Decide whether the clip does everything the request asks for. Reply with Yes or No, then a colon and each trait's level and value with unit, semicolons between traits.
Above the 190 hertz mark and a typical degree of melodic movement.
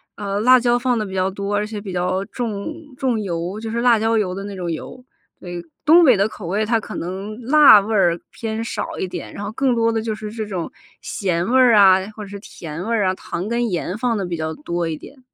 Yes: high, 210 Hz; average, 3.6 semitones